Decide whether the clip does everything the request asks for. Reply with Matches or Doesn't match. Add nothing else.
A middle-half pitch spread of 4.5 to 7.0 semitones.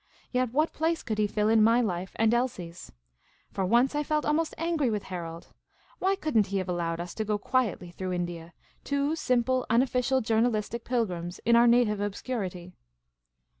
Matches